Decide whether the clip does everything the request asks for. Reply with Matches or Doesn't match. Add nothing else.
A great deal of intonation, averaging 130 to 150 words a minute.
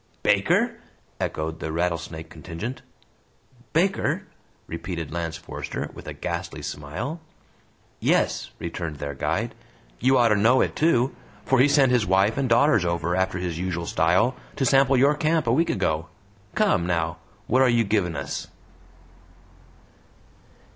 Matches